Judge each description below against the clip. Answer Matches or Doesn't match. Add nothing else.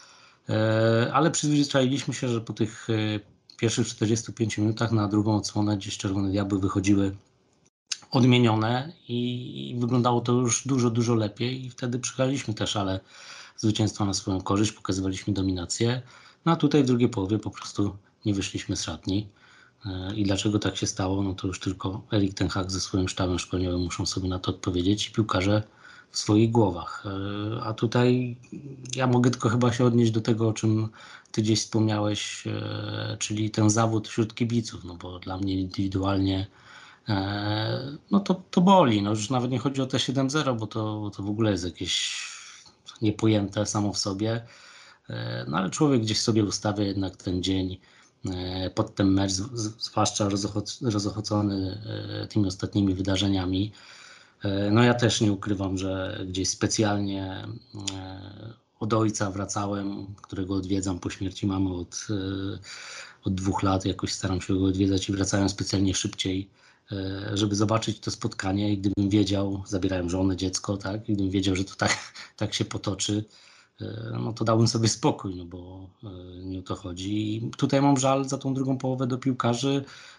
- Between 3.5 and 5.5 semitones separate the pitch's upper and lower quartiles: Doesn't match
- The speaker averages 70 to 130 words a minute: Doesn't match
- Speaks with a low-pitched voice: Matches